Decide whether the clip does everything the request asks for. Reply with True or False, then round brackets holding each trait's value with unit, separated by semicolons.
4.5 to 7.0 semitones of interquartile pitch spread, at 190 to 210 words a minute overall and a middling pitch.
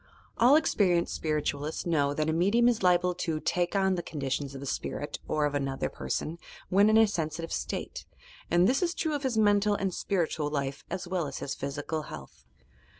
True (5.4 semitones; 200 wpm; 170 Hz)